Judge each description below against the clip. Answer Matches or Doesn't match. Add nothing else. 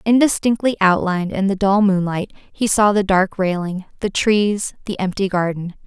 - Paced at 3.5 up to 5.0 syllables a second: Matches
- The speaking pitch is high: Matches